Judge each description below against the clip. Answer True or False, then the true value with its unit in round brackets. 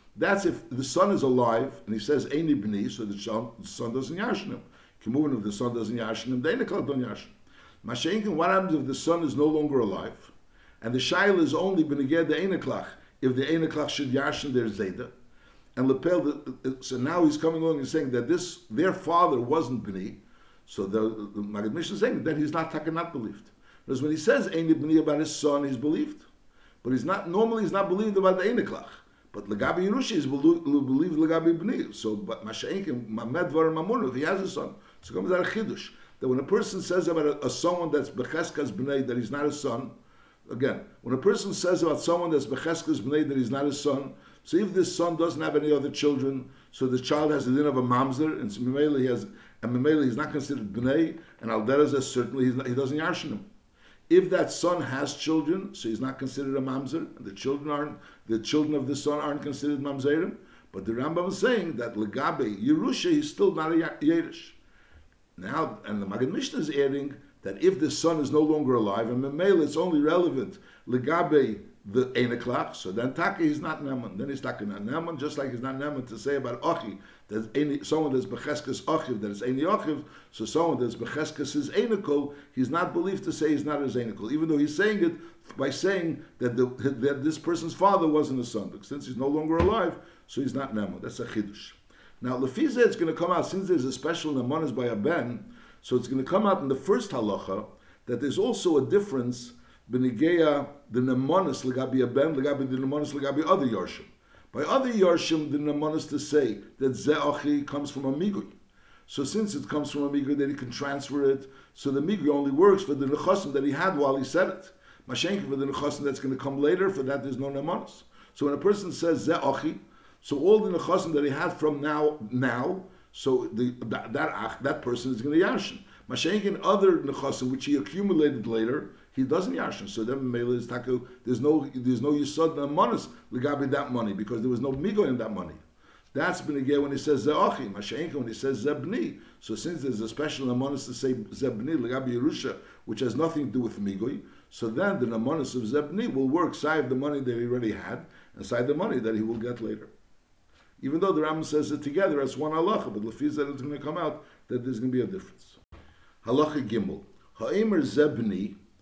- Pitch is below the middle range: False (145 Hz)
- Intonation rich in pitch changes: False (4.0 semitones)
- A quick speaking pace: True (215 wpm)